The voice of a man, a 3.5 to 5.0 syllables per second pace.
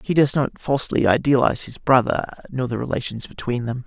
No: male; 5.7 syllables/s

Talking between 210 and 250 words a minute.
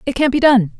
No: fast, 305 wpm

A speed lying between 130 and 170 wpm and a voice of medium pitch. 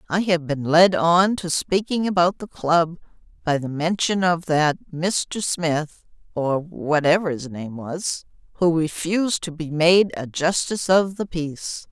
Yes: average, 160 wpm; medium, 165 Hz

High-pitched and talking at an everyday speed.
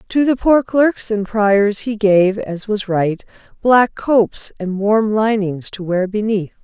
Yes: high, 210 Hz; average, 170 wpm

